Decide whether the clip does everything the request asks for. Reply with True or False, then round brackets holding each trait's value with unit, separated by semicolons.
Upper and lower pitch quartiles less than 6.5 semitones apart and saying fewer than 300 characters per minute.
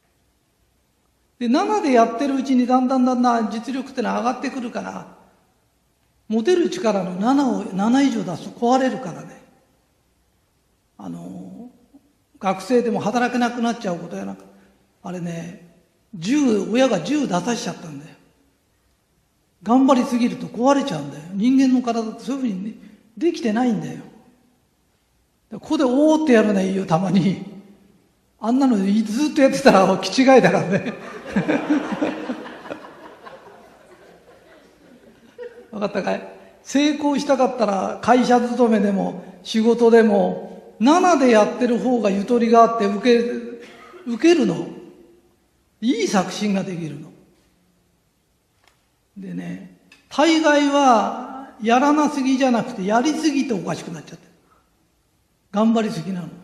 True (5.3 semitones; 265 characters per minute)